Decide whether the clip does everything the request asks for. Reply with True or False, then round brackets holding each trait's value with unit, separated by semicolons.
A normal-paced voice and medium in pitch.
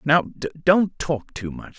True (170 wpm; 150 Hz)